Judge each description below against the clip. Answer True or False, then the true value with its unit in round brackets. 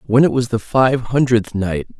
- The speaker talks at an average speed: False (210 wpm)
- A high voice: False (120 Hz)